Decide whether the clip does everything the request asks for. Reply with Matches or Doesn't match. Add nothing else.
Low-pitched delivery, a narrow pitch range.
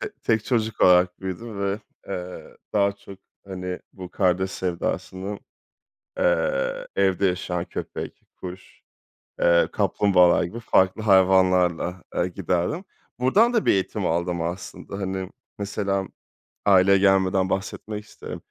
Matches